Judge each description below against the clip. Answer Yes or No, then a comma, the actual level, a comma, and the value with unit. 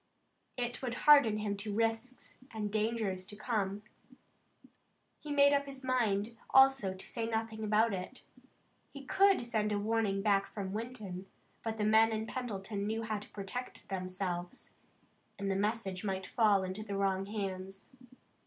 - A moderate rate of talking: Yes, average, 155 wpm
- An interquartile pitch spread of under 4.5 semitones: Yes, average, 2.8 semitones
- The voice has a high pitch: Yes, high, 215 Hz